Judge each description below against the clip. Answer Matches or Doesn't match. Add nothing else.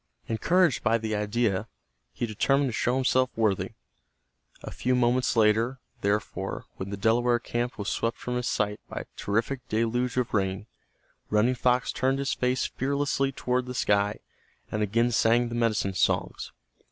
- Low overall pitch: Matches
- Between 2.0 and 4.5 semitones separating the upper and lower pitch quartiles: Matches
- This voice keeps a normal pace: Matches